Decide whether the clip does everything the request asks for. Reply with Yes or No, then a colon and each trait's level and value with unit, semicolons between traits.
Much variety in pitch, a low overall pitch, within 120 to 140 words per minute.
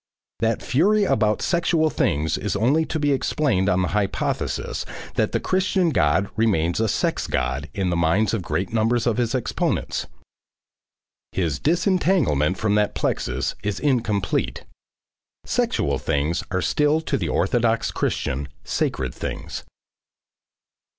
Yes: wide, 8.7 semitones; low, 110 Hz; slow, 135 wpm